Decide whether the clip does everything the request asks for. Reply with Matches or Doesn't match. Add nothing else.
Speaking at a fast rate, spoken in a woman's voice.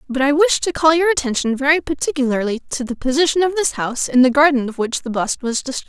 Matches